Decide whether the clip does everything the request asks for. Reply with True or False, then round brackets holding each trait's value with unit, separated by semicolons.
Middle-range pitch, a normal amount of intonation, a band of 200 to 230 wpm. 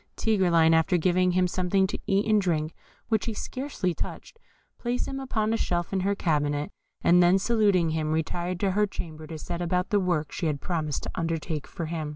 True (180 Hz; 3.7 semitones; 205 wpm)